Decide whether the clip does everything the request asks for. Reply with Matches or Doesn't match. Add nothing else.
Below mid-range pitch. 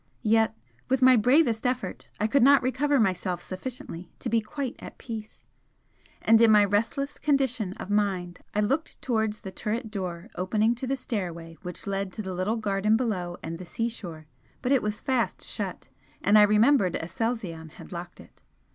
Doesn't match